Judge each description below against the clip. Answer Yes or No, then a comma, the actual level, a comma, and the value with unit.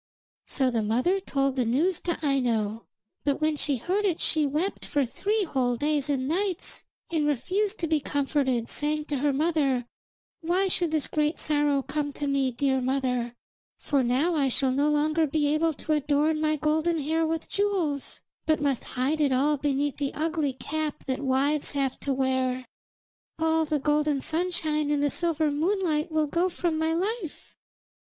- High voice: Yes, very high, 295 Hz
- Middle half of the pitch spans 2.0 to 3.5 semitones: Yes, average, 2.7 semitones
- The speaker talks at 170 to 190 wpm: Yes, average, 175 wpm